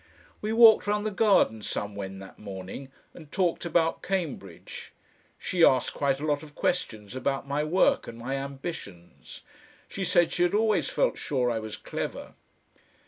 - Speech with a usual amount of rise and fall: No, wide, 8.4 semitones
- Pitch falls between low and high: Yes, medium, 145 Hz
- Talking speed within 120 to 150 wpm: No, average, 160 wpm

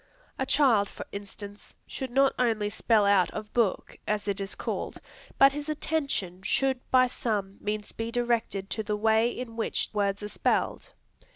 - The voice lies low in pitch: No, high, 220 Hz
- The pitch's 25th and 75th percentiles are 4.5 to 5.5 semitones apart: No, average, 3.6 semitones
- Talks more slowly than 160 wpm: No, average, 170 wpm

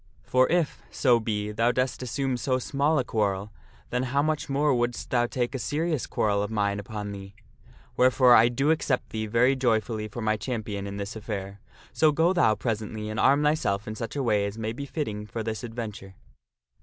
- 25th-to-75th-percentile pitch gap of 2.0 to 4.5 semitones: Yes, average, 4.0 semitones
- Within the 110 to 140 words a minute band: No, average, 200 wpm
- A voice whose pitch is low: Yes, low, 115 Hz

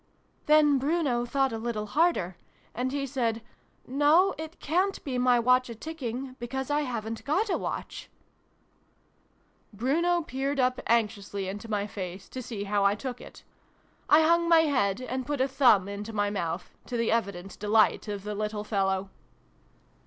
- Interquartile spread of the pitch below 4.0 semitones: No, wide, 5.4 semitones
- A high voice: Yes, high, 245 Hz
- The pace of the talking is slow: No, average, 170 wpm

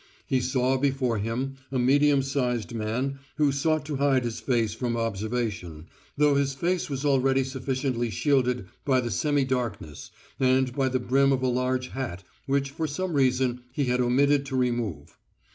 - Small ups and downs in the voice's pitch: Yes, narrow, 2.2 semitones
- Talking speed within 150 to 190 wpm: Yes, average, 170 wpm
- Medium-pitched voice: No, low, 130 Hz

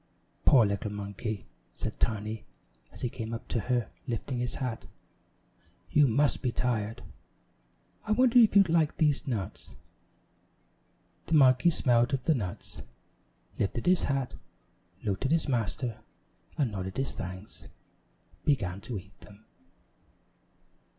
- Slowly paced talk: Yes, slow, 130 wpm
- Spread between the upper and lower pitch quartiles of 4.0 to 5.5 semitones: Yes, average, 5.2 semitones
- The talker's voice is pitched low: Yes, low, 120 Hz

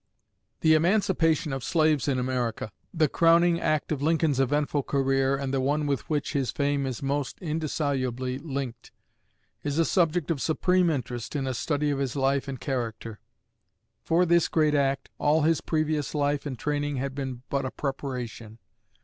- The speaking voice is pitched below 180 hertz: Yes, medium, 140 Hz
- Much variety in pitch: No, average, 2.7 semitones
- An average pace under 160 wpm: No, average, 165 wpm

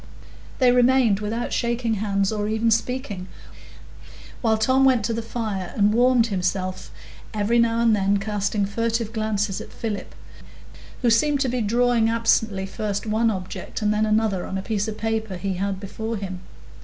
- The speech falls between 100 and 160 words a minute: No, average, 170 wpm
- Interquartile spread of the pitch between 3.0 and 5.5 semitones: No, narrow, 2.5 semitones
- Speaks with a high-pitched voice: Yes, high, 220 Hz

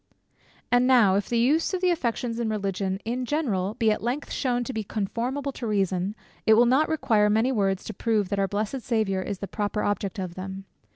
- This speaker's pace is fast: Yes, fast, 215 wpm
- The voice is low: No, high, 220 Hz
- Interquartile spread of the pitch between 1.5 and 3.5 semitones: No, average, 3.9 semitones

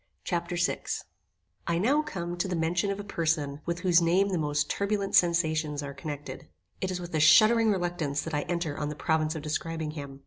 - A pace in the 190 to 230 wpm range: Yes, fast, 205 wpm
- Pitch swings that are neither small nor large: Yes, average, 3.0 semitones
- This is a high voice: No, medium, 170 Hz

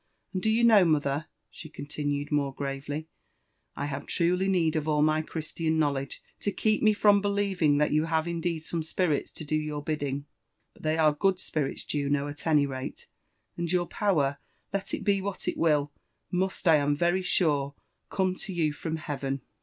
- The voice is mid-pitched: Yes, medium, 155 Hz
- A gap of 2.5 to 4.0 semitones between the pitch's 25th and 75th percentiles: Yes, average, 3.7 semitones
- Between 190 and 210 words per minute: Yes, average, 195 wpm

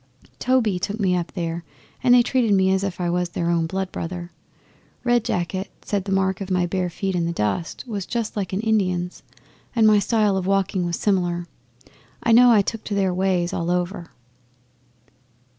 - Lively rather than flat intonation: No, average, 2.9 semitones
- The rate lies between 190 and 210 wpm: Yes, average, 195 wpm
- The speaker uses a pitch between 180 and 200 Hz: Yes, high, 190 Hz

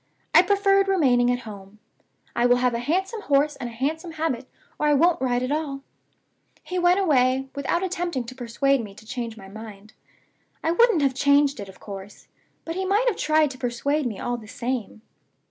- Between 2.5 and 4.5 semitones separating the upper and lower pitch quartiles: No, wide, 5.5 semitones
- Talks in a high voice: Yes, very high, 270 Hz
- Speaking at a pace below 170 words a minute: No, average, 195 wpm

